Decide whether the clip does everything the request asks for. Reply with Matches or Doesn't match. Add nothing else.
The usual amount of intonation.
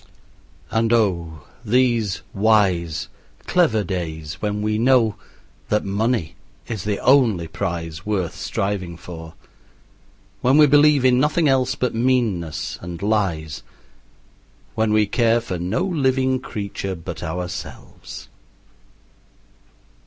Doesn't match